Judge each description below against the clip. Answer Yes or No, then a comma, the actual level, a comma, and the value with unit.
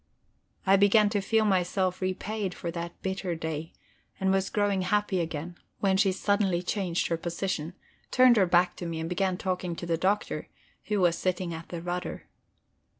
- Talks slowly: No, average, 175 wpm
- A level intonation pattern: Yes, narrow, 2.3 semitones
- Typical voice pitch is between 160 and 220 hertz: Yes, medium, 185 Hz